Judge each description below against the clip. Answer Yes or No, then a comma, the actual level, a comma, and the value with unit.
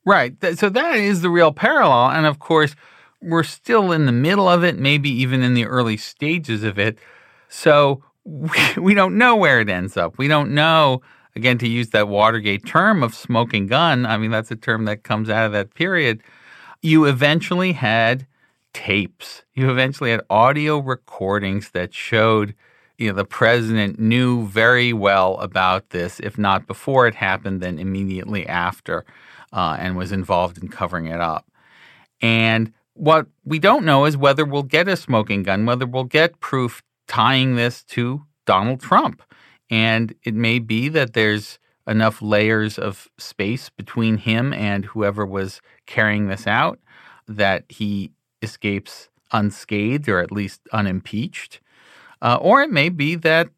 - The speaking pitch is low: Yes, low, 115 Hz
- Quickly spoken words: No, average, 160 wpm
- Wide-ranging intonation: Yes, wide, 5.9 semitones